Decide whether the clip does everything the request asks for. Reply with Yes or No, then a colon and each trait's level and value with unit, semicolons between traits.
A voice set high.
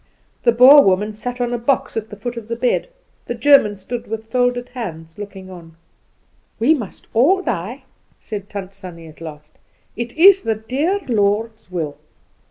Yes: high, 225 Hz